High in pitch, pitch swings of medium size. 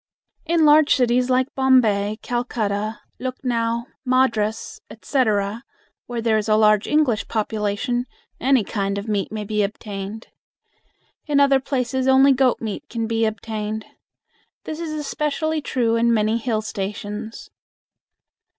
Yes: high, 230 Hz; average, 3.5 semitones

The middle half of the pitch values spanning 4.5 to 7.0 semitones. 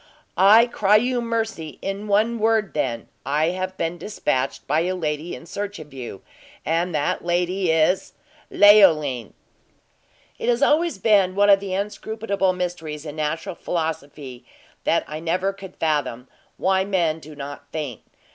Yes: average, 4.9 semitones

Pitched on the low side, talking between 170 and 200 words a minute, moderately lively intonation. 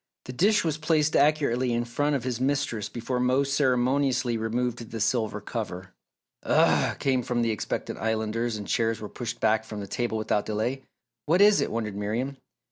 Yes: low, 120 Hz; average, 175 wpm; average, 3.6 semitones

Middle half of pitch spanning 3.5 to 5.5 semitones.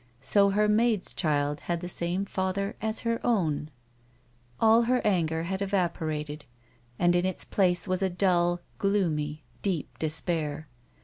Yes: average, 3.9 semitones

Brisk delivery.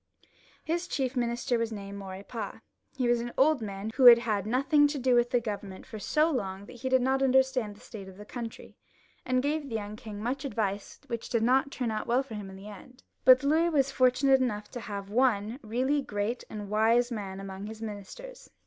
Yes: fast, 215 wpm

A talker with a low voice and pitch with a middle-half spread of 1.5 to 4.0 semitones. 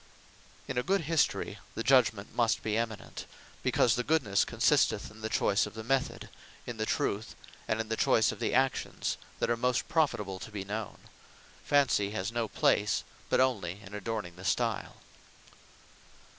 Yes: low, 110 Hz; average, 3.4 semitones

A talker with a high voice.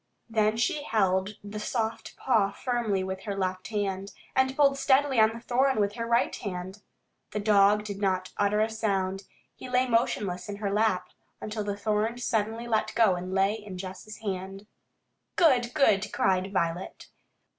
Yes: high, 210 Hz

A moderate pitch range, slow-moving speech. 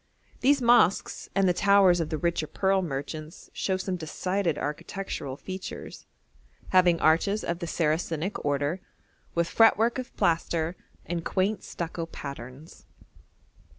Yes: average, 3.5 semitones; slow, 125 wpm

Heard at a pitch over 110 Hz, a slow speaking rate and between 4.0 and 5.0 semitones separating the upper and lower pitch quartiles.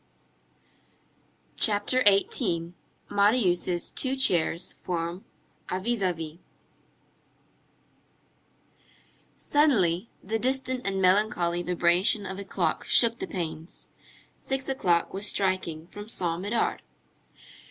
Yes: high, 190 Hz; slow, 95 wpm; average, 4.5 semitones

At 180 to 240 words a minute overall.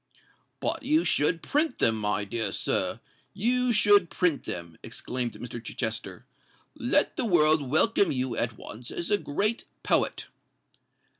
No: slow, 135 wpm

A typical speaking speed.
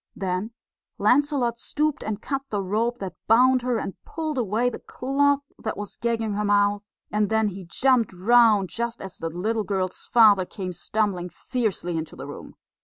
Yes: average, 175 wpm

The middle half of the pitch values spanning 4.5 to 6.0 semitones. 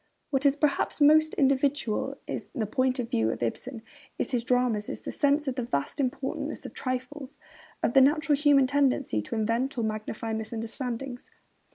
No: average, 3.6 semitones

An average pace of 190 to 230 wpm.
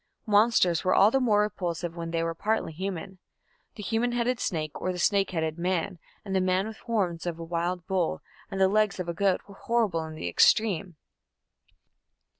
Yes: average, 200 wpm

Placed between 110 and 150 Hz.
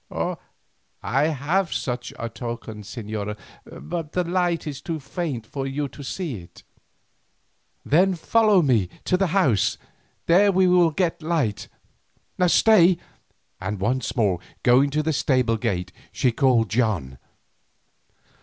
Yes: medium, 140 Hz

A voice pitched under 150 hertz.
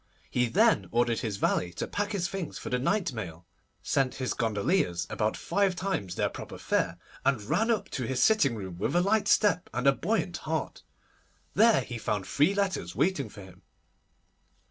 Yes: low, 135 Hz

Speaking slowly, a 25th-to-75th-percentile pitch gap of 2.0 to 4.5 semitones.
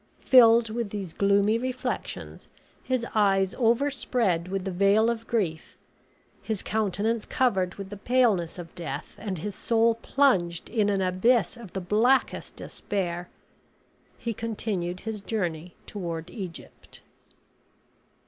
Yes: slow, 125 wpm; average, 4.0 semitones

